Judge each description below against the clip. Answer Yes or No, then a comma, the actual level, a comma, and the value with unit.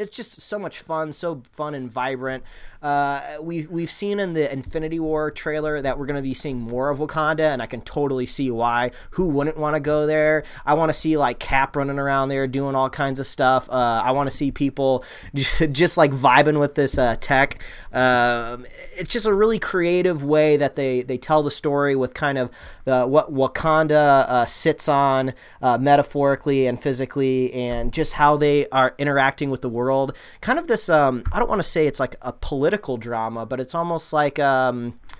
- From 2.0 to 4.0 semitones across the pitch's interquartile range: Yes, average, 2.9 semitones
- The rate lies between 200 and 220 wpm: Yes, fast, 205 wpm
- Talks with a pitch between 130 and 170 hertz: Yes, medium, 140 Hz